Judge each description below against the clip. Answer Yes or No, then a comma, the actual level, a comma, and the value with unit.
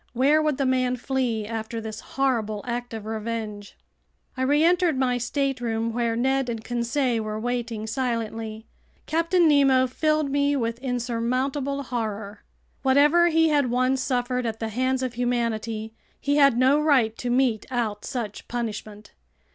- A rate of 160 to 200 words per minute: No, average, 145 wpm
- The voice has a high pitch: Yes, high, 245 Hz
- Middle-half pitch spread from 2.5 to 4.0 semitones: Yes, average, 3.2 semitones